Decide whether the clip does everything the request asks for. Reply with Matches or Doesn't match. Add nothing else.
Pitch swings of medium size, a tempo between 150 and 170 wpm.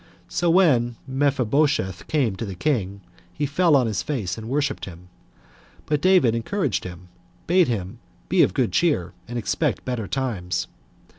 Doesn't match